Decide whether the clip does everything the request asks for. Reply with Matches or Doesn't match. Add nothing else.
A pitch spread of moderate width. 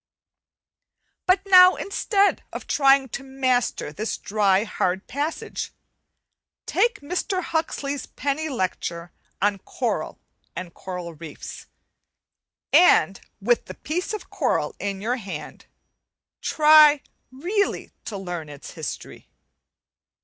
Doesn't match